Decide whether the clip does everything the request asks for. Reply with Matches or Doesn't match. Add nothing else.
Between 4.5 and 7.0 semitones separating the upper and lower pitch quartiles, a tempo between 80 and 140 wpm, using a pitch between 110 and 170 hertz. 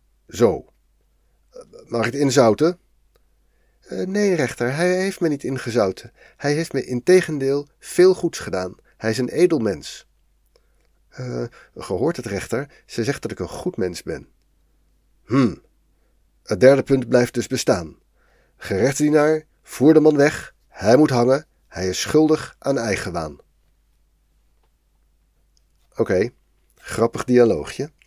Matches